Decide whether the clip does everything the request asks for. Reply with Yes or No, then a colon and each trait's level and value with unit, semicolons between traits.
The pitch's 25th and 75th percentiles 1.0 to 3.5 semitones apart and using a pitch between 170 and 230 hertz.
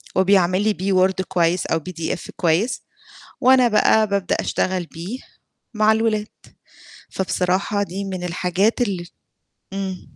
Yes: average, 2.8 semitones; high, 190 Hz